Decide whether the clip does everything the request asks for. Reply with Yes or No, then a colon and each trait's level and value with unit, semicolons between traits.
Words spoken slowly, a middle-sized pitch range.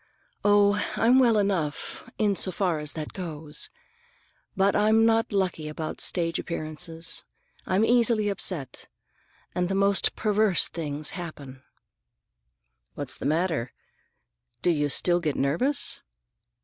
Yes: slow, 125 wpm; average, 4.9 semitones